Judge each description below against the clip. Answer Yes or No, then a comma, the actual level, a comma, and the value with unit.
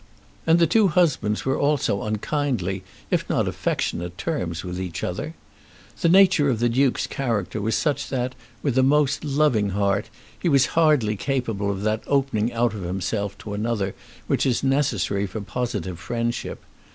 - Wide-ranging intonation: Yes, wide, 5.8 semitones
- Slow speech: No, average, 165 wpm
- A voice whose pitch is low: Yes, low, 115 Hz